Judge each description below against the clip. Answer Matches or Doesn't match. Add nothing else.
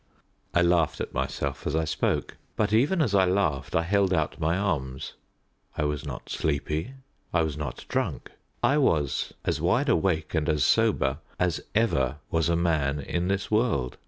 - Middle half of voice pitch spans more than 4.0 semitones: Matches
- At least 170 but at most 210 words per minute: Matches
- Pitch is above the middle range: Doesn't match